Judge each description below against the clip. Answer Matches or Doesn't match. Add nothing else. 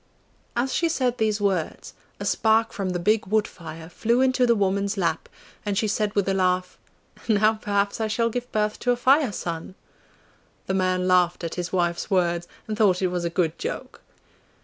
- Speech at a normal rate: Matches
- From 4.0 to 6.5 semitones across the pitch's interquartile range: Doesn't match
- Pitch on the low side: Doesn't match